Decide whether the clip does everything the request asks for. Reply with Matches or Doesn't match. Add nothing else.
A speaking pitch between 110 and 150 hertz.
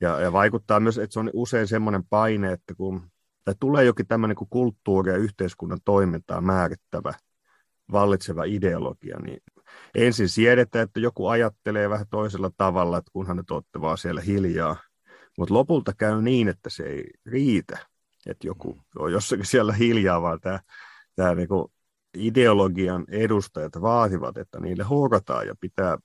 Doesn't match